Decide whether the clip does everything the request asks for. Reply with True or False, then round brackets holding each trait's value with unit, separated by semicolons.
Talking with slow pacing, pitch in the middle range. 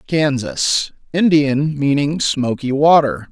True (70 wpm; 145 Hz)